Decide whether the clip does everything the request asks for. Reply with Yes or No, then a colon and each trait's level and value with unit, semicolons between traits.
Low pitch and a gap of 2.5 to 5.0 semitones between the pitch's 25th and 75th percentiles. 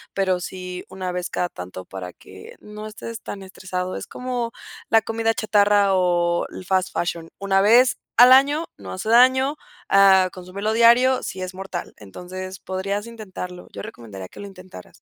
No: high, 190 Hz; average, 3.6 semitones